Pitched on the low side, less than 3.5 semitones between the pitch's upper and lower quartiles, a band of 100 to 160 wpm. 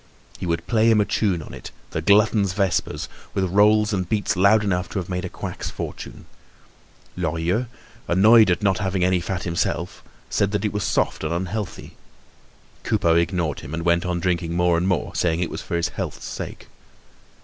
No: very low, 90 Hz; average, 3.1 semitones; average, 190 wpm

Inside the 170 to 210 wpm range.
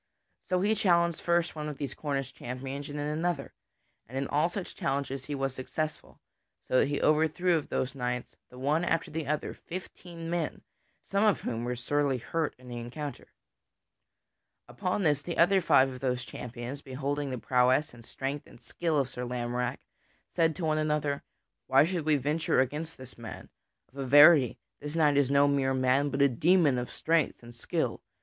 Yes: average, 185 wpm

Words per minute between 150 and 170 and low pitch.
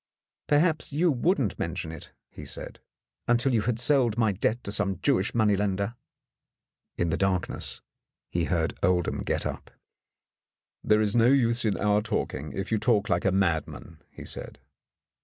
Yes: average, 160 wpm; low, 105 Hz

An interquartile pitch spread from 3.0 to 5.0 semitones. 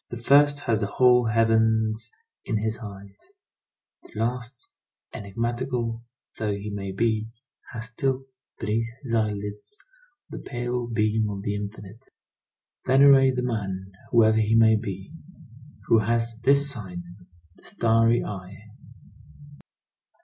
No: narrow, 2.6 semitones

